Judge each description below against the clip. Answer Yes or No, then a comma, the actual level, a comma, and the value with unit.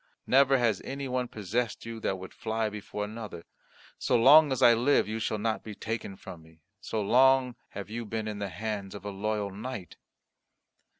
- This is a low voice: Yes, low, 110 Hz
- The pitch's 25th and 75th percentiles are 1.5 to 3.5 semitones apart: Yes, average, 3.2 semitones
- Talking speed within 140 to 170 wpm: No, average, 190 wpm